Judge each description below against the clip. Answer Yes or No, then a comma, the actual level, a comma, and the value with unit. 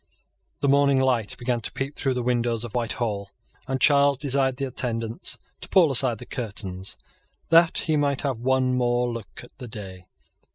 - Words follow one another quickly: No, average, 175 wpm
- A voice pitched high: No, low, 125 Hz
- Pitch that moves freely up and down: No, average, 3.0 semitones